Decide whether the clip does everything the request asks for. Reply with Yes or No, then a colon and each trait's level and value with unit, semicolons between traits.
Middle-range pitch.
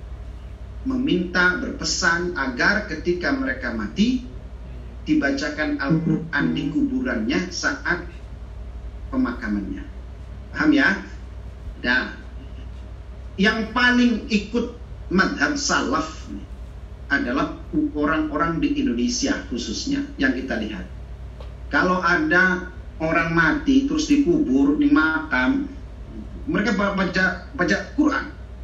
Yes: medium, 165 Hz